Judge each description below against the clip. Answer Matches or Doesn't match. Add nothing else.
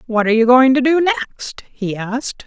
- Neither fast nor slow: Doesn't match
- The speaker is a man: Doesn't match